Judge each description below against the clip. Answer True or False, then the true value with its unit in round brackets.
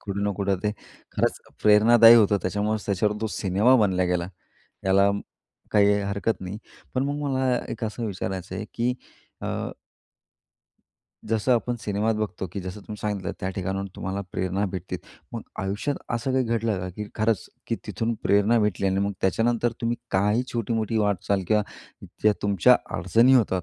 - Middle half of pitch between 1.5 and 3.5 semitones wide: True (2.8 semitones)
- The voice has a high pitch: False (105 Hz)